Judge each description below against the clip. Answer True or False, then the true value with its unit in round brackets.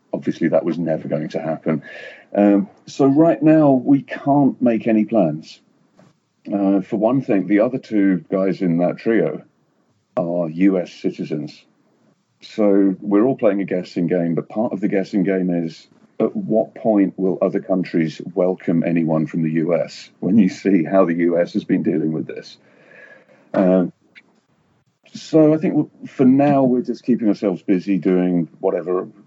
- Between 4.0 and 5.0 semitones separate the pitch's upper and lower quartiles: True (4.3 semitones)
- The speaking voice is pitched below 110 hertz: True (95 Hz)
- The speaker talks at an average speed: False (160 wpm)